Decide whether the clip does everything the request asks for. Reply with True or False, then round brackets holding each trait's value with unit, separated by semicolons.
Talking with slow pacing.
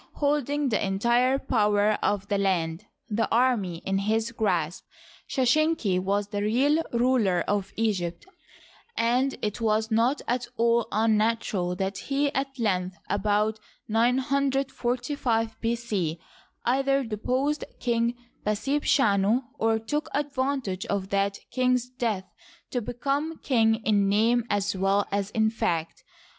True (125 wpm)